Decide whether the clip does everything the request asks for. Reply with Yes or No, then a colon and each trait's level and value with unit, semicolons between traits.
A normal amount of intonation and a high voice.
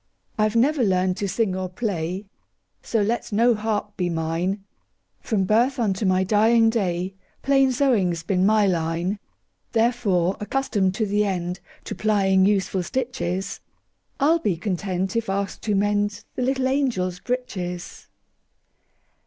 Yes: average, 3.8 semitones; high, 200 Hz